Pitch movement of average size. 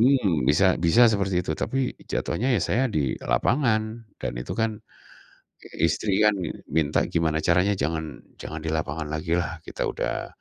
No: wide, 5.7 semitones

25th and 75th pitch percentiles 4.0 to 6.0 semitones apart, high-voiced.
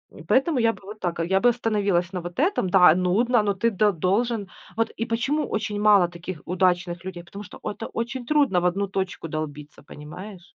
Yes: average, 4.3 semitones; high, 195 Hz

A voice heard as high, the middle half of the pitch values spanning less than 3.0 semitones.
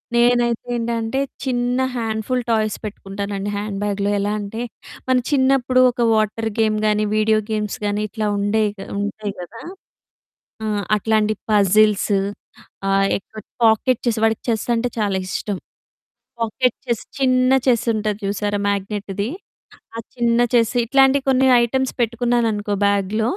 Yes: high, 220 Hz; narrow, 2.6 semitones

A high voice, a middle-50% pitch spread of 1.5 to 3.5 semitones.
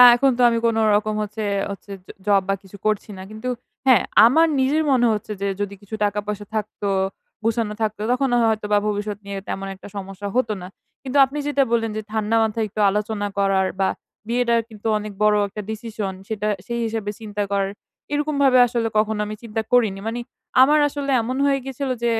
Yes: high, 220 Hz; average, 2.7 semitones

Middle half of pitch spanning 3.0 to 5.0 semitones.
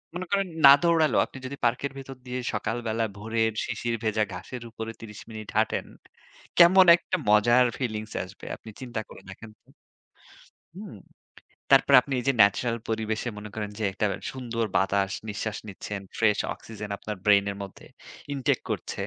Yes: average, 3.3 semitones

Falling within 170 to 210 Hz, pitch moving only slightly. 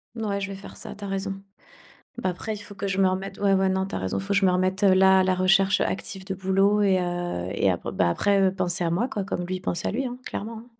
Yes: high, 190 Hz; narrow, 1.3 semitones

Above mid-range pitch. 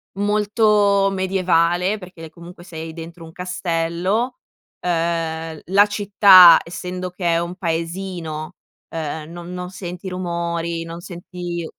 No: medium, 175 Hz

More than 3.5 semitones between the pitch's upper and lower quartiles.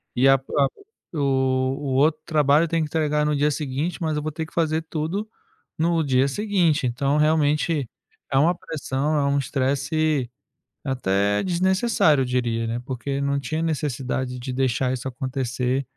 No: average, 3.1 semitones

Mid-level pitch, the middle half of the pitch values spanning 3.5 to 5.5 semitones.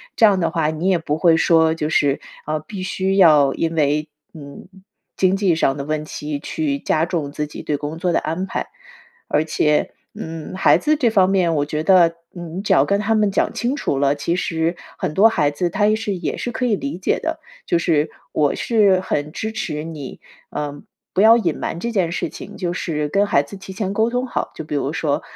Yes: medium, 170 Hz; average, 4.7 semitones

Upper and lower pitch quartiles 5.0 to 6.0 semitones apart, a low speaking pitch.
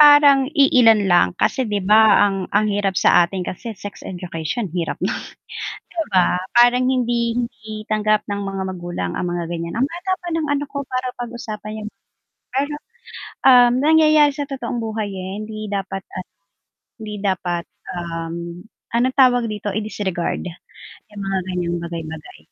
No: average, 5.3 semitones; high, 210 Hz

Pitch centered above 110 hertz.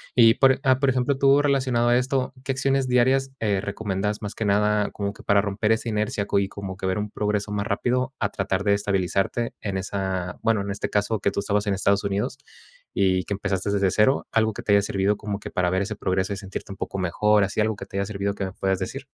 No: low, 105 Hz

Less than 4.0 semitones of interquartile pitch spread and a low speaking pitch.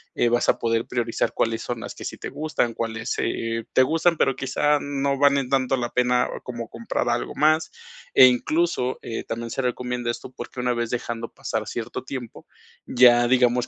Yes: narrow, 2.4 semitones; low, 125 Hz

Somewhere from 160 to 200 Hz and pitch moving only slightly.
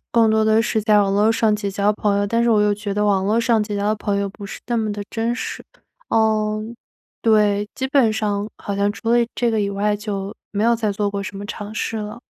No: high, 210 Hz; narrow, 1.5 semitones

